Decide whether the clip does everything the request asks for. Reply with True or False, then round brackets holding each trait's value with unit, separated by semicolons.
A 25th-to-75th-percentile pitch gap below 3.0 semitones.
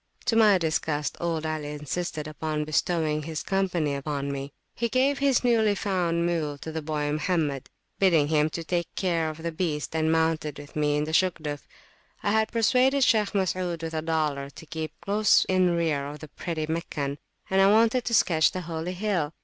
False (3.8 semitones)